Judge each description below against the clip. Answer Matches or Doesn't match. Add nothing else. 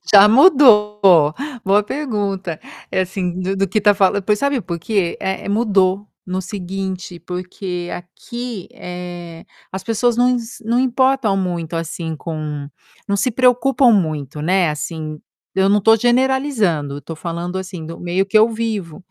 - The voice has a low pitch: Doesn't match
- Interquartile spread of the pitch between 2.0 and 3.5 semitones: Doesn't match